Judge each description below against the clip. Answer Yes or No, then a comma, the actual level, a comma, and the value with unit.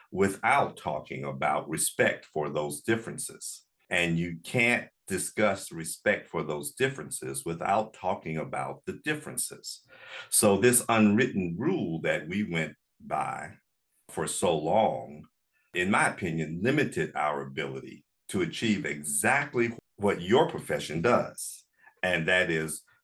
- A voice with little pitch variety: No, wide, 5.6 semitones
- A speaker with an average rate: No, slow, 120 wpm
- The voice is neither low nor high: No, very low, 85 Hz